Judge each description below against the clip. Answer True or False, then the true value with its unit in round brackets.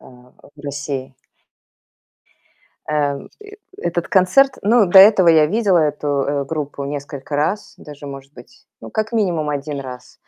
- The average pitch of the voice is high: False (150 Hz)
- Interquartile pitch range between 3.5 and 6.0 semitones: True (4.8 semitones)